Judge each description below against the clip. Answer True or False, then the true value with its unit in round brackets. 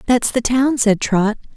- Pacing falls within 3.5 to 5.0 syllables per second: True (4.1 syllables/s)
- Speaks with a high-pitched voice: True (235 Hz)